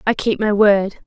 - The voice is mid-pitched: No, high, 205 Hz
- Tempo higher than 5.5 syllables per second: No, 4.8 syllables/s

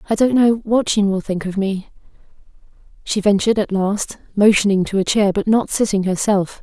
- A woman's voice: Yes, female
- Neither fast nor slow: Yes, average, 190 wpm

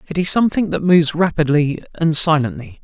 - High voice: No, medium, 160 Hz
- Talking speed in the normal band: Yes, average, 170 wpm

